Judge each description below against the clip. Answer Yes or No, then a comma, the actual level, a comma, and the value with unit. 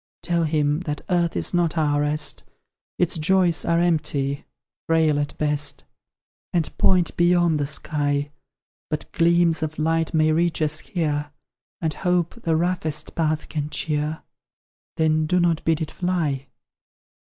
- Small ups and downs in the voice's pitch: Yes, narrow, 2.3 semitones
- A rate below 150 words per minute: Yes, average, 140 wpm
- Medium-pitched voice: Yes, medium, 160 Hz